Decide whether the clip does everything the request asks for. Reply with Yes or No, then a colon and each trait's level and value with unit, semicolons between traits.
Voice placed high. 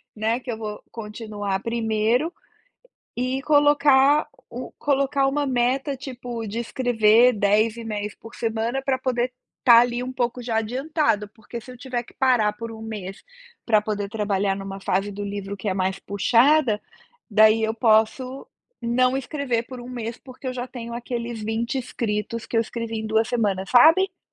Yes: high, 230 Hz